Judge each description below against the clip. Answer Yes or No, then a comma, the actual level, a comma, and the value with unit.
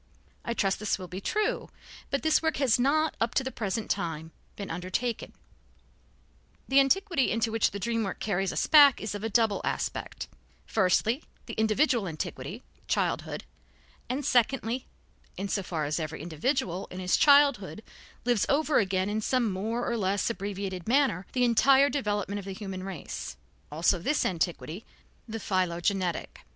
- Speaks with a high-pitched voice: Yes, high, 215 Hz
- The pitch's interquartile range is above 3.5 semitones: Yes, average, 5.3 semitones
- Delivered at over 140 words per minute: Yes, average, 160 wpm